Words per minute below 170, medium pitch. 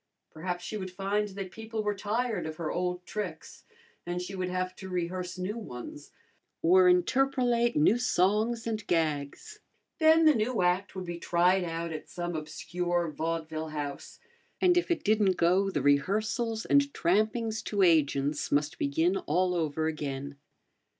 Yes: average, 155 wpm; medium, 180 Hz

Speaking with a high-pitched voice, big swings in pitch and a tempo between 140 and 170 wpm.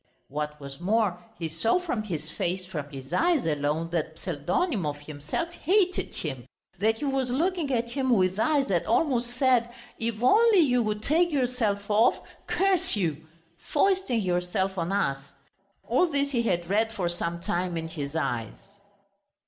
Yes: high, 205 Hz; wide, 8.1 semitones; average, 160 wpm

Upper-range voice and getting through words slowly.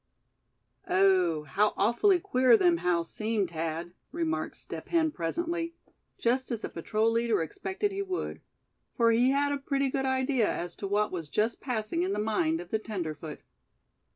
No: high, 225 Hz; average, 165 wpm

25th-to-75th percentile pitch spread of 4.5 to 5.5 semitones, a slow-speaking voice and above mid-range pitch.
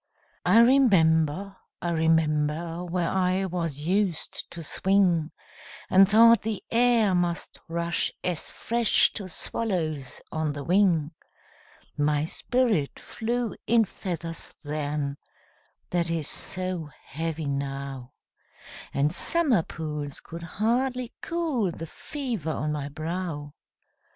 No: average, 5.2 semitones; slow, 110 wpm; medium, 170 Hz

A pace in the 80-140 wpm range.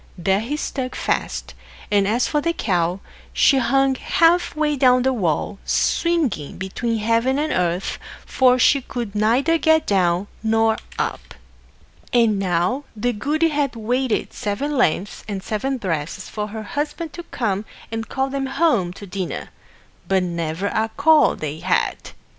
No: average, 155 wpm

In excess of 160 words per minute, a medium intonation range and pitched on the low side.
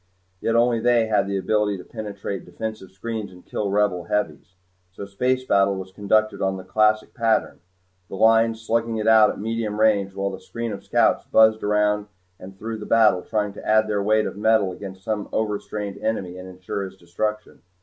No: average, 195 wpm; narrow, 2.2 semitones; low, 105 Hz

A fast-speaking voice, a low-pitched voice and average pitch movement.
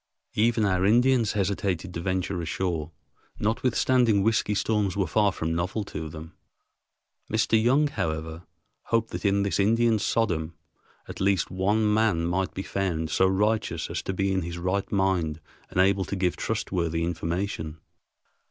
No: average, 150 wpm; very low, 95 Hz; average, 3.8 semitones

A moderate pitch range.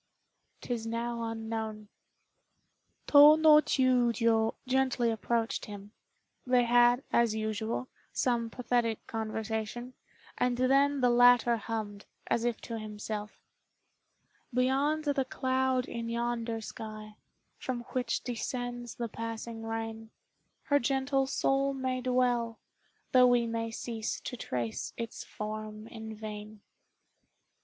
No: narrow, 2.3 semitones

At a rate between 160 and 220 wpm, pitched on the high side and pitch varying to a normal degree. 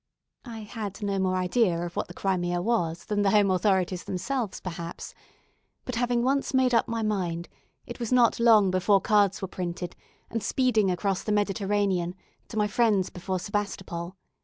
Yes: average, 170 wpm; high, 200 Hz; average, 3.5 semitones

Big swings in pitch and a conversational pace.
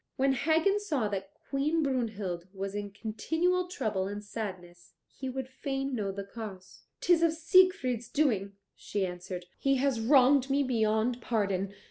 Yes: wide, 5.8 semitones; average, 150 wpm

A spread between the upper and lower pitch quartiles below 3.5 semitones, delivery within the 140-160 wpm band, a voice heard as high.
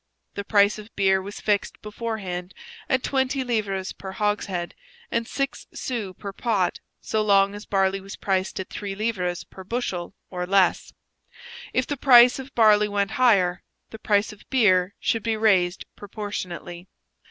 Yes: average, 2.9 semitones; average, 155 wpm; high, 205 Hz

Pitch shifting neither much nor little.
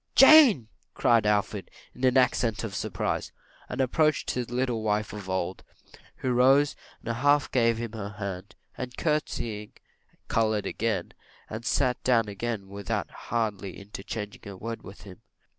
Yes: average, 3.5 semitones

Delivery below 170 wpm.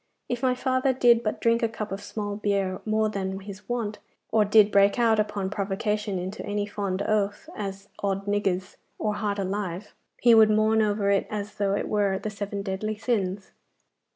No: average, 185 wpm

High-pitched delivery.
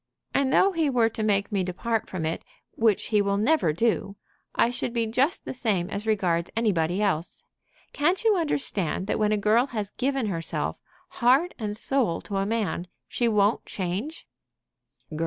Yes: high, 215 Hz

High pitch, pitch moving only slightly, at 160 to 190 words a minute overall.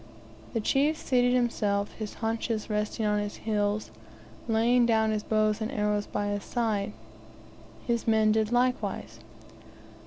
No: high, 220 Hz; narrow, 2.1 semitones; slow, 135 wpm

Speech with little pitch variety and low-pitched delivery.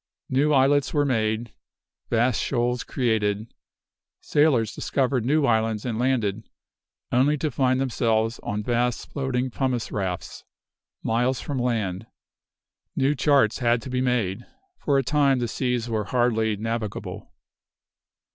No: average, 3.0 semitones; low, 120 Hz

